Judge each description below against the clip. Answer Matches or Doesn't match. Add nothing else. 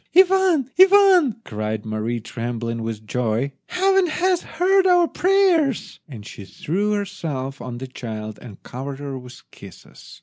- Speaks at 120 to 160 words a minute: Matches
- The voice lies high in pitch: Doesn't match